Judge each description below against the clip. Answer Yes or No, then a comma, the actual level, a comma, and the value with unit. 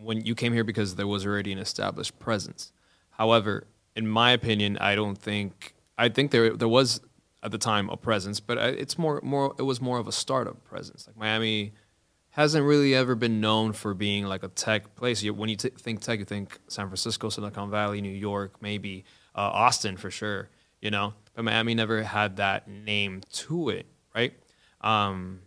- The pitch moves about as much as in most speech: No, narrow, 2.3 semitones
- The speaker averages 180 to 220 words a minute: Yes, average, 190 wpm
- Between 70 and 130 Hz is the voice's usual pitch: Yes, low, 110 Hz